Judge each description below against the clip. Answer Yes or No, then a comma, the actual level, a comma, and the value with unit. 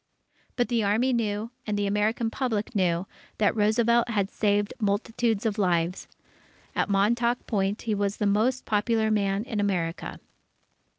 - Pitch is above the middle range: Yes, high, 210 Hz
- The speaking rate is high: No, average, 150 wpm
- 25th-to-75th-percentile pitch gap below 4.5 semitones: Yes, narrow, 2.4 semitones